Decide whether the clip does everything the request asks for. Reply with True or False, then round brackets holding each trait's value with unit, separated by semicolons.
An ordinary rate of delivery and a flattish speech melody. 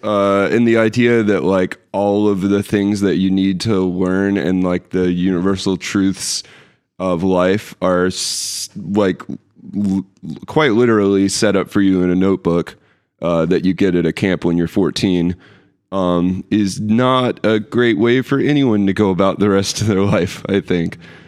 True (180 wpm; 2.2 semitones)